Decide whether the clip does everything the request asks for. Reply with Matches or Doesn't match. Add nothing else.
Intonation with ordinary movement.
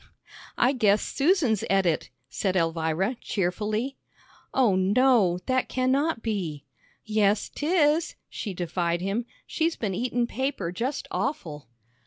Doesn't match